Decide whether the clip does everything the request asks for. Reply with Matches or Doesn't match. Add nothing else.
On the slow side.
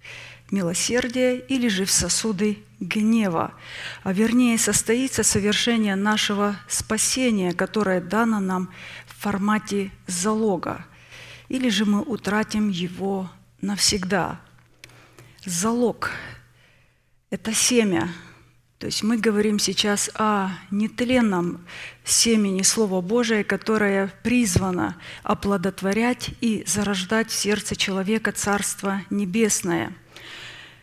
Matches